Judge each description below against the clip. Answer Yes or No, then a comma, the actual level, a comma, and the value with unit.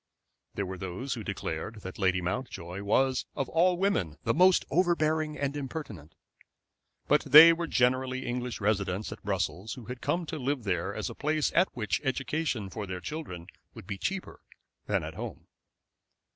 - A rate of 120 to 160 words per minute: No, average, 170 wpm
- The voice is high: No, low, 125 Hz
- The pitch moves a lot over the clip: Yes, wide, 8.0 semitones